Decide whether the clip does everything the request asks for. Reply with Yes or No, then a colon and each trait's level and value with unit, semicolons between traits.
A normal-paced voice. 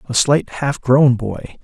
Yes: average, 185 wpm